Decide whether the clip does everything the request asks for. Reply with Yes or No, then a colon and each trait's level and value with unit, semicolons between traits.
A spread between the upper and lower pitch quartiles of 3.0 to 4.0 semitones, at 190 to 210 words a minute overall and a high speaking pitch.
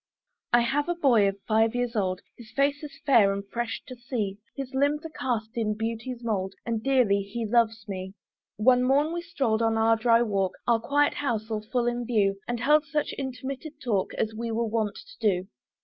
Yes: average, 3.5 semitones; fast, 205 wpm; high, 235 Hz